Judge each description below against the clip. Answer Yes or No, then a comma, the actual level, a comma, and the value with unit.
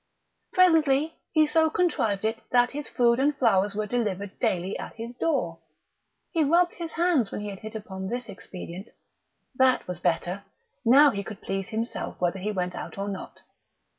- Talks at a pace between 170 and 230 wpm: Yes, average, 175 wpm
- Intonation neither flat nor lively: No, wide, 6.6 semitones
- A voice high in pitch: Yes, high, 225 Hz